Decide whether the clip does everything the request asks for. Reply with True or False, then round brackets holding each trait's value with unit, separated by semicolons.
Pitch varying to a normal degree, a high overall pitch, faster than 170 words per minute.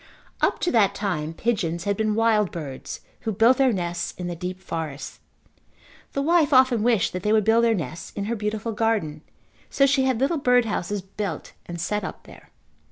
True (4.9 semitones; 210 Hz; 195 wpm)